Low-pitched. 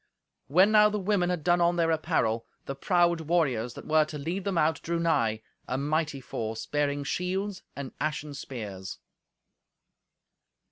No: medium, 155 Hz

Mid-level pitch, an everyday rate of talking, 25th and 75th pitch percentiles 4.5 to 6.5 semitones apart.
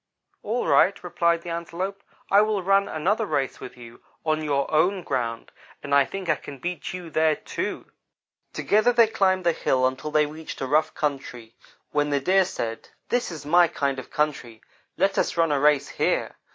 Yes: medium, 155 Hz; average, 190 wpm; average, 5.0 semitones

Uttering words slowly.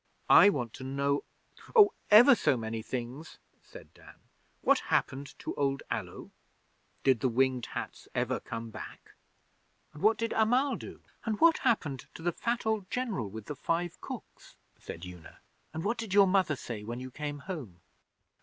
No: average, 170 wpm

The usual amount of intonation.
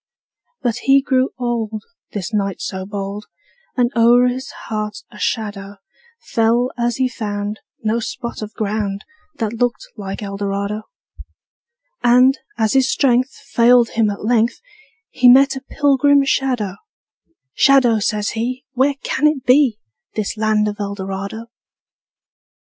Yes: average, 3.4 semitones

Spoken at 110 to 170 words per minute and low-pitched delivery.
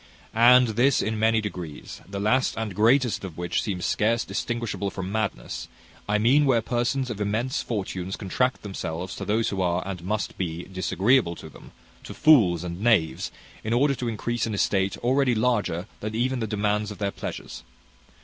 No: average, 180 wpm; low, 105 Hz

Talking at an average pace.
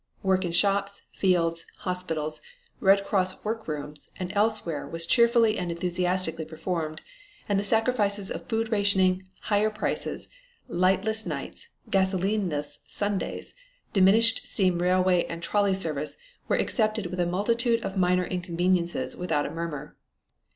No: slow, 130 wpm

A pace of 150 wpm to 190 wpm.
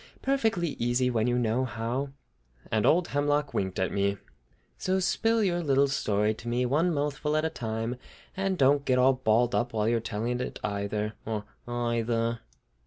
Yes: average, 175 wpm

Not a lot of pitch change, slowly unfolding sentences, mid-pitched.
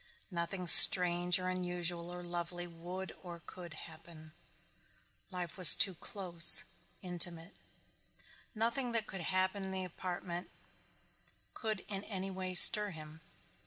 Yes: narrow, 1.7 semitones; slow, 125 wpm; medium, 180 Hz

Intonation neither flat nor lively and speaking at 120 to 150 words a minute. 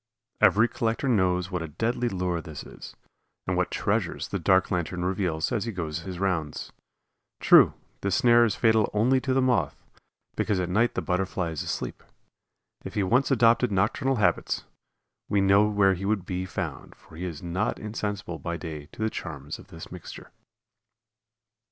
No: average, 4.2 semitones; average, 175 wpm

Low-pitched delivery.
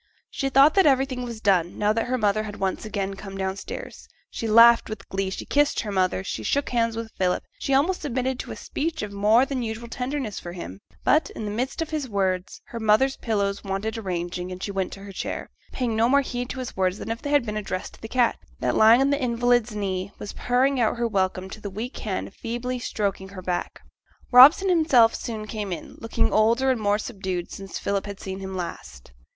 No: high, 220 Hz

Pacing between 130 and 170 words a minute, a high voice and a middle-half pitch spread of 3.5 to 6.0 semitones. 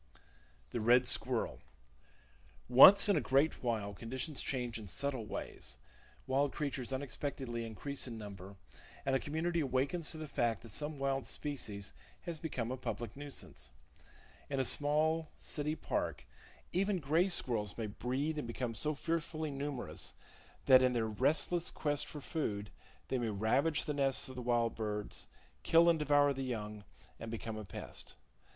No: average, 160 wpm; low, 130 Hz; average, 4.5 semitones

